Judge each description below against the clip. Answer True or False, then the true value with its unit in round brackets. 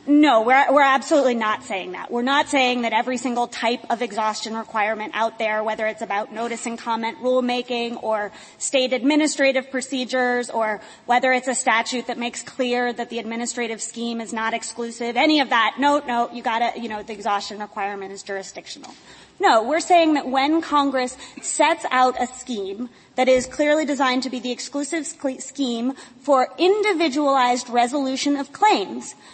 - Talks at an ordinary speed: True (170 wpm)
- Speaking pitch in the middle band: False (245 Hz)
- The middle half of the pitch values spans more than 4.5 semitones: False (3.2 semitones)